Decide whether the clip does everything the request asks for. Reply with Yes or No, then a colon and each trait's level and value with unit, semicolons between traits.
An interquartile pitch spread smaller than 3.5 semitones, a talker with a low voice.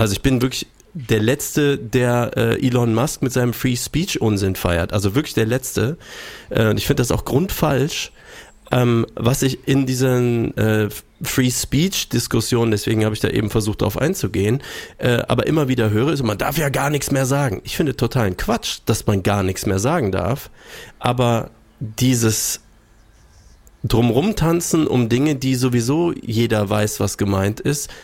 No: average, 3.9 semitones; low, 120 Hz